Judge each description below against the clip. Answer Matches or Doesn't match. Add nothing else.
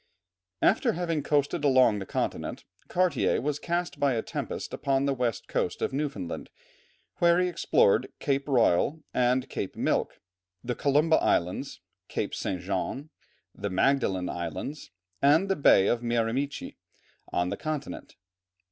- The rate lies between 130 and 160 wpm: Matches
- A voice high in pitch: Doesn't match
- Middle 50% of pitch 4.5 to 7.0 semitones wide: Matches